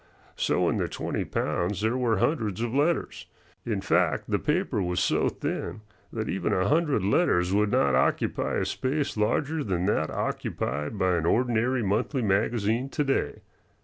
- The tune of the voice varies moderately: No, wide, 5.8 semitones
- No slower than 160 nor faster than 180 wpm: Yes, average, 165 wpm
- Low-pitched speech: Yes, low, 105 Hz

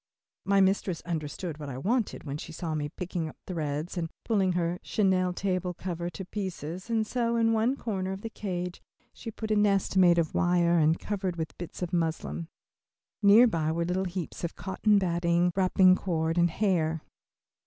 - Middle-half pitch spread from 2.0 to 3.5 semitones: Yes, average, 2.9 semitones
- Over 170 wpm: Yes, average, 185 wpm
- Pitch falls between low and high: Yes, medium, 180 Hz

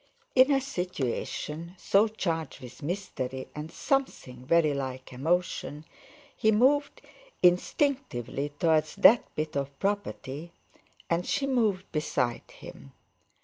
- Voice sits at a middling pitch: Yes, medium, 170 Hz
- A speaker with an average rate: No, slow, 110 wpm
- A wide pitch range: Yes, wide, 6.8 semitones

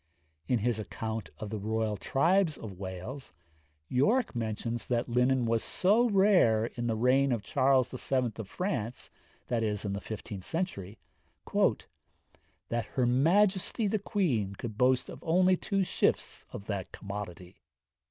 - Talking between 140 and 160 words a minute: Yes, average, 145 wpm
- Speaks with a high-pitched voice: No, low, 120 Hz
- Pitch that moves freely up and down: Yes, wide, 7.0 semitones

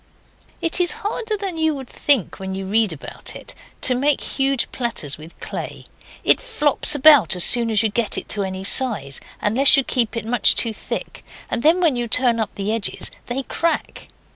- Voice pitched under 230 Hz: No, high, 240 Hz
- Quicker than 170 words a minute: Yes, average, 190 wpm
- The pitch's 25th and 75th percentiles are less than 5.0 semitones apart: No, wide, 5.6 semitones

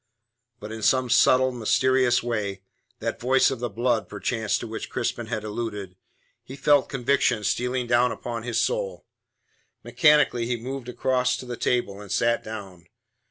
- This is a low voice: Yes, low, 120 Hz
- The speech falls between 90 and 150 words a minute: No, average, 160 wpm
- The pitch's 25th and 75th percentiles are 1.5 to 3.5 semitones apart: Yes, average, 2.8 semitones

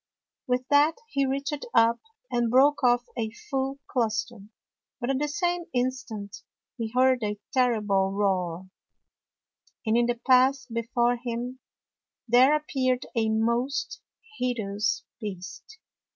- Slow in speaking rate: Yes, slow, 125 wpm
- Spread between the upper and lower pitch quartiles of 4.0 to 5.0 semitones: No, average, 3.0 semitones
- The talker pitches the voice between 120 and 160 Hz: No, high, 245 Hz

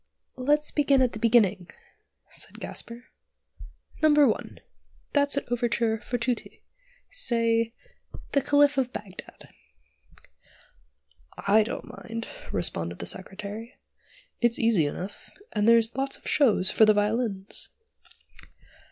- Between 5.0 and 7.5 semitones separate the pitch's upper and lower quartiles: No, average, 3.8 semitones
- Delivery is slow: Yes, slow, 115 wpm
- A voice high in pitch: Yes, high, 230 Hz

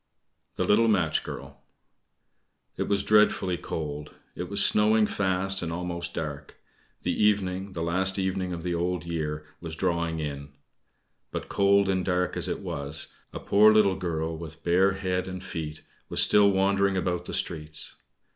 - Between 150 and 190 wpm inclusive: Yes, average, 160 wpm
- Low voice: Yes, very low, 90 Hz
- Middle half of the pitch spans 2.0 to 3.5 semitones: Yes, average, 3.0 semitones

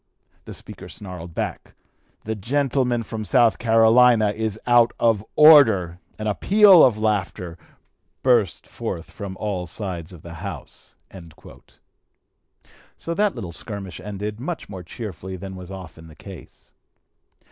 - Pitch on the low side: Yes, low, 105 Hz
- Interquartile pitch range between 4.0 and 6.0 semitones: Yes, average, 4.5 semitones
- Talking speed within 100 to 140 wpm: Yes, slow, 135 wpm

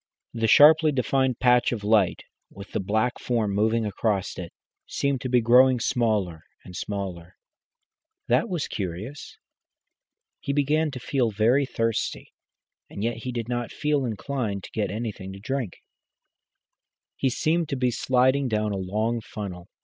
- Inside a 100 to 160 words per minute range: Yes, average, 150 wpm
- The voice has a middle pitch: No, low, 115 Hz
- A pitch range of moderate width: Yes, average, 4.3 semitones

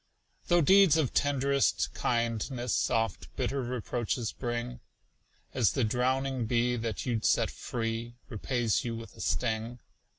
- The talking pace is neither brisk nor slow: No, slow, 130 wpm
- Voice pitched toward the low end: Yes, low, 120 Hz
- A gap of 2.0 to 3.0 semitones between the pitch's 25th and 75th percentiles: Yes, narrow, 2.5 semitones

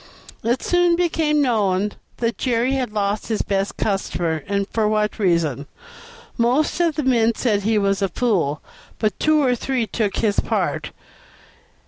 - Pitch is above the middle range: Yes, high, 220 Hz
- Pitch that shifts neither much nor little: Yes, average, 4.5 semitones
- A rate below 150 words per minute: No, average, 155 wpm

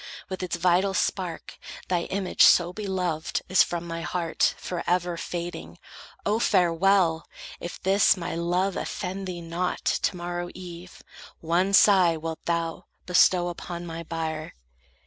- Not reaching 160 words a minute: Yes, slow, 135 wpm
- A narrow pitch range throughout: Yes, narrow, 1.7 semitones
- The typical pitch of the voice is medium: Yes, medium, 175 Hz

